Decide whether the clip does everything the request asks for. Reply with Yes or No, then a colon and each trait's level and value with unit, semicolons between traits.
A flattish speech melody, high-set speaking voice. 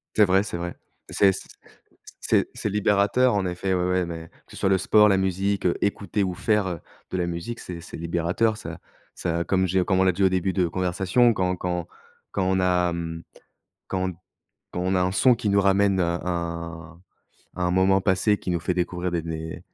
No: narrow, 2.0 semitones; very low, 90 Hz